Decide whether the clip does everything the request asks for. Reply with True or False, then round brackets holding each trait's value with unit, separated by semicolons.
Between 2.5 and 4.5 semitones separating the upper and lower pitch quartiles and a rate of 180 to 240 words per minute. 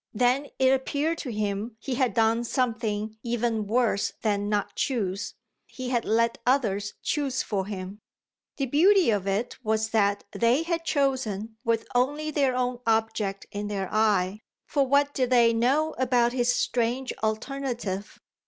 False (3.7 semitones; 155 wpm)